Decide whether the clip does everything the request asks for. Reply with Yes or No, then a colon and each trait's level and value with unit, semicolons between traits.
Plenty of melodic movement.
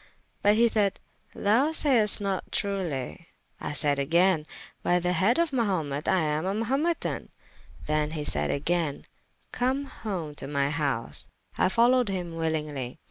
Yes: wide, 6.5 semitones